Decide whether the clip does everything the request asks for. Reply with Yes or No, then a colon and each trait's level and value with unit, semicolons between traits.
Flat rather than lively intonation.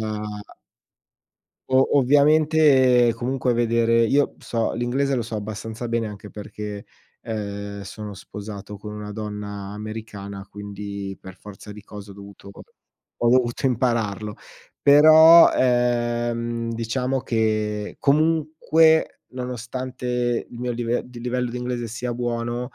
No: average, 3.1 semitones